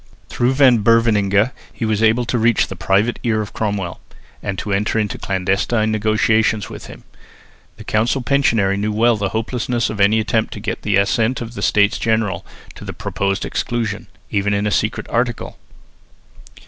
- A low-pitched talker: Yes, low, 110 Hz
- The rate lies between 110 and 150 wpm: No, average, 175 wpm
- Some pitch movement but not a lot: No, narrow, 2.3 semitones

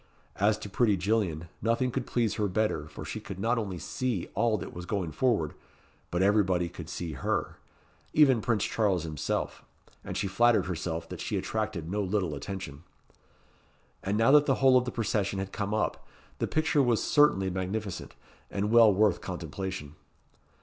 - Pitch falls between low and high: No, low, 100 Hz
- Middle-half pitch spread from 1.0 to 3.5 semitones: No, average, 4.1 semitones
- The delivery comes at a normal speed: Yes, average, 170 wpm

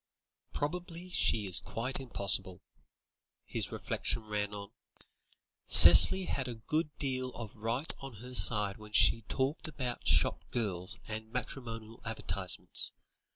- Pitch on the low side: Yes, low, 115 Hz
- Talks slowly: Yes, slow, 125 wpm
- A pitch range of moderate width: Yes, average, 4.2 semitones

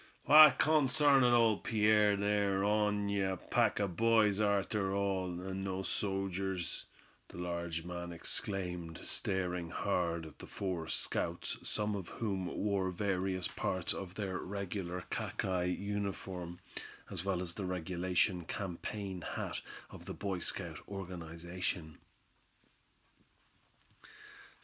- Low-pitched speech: Yes, very low, 95 Hz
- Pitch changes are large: No, narrow, 2.5 semitones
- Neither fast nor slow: No, slow, 120 wpm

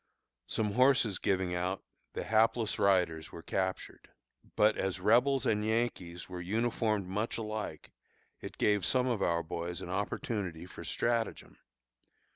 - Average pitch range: Yes, average, 3.9 semitones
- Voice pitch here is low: Yes, low, 100 Hz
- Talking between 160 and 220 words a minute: No, slow, 135 wpm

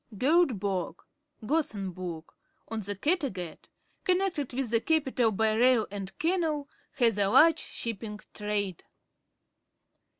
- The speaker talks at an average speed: No, slow, 105 wpm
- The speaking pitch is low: No, high, 225 Hz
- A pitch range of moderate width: No, wide, 6.8 semitones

